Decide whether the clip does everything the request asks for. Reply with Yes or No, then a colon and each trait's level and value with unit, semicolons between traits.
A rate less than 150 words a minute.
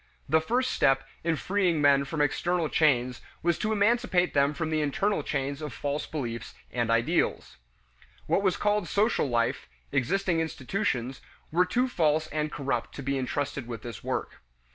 No: average, 165 wpm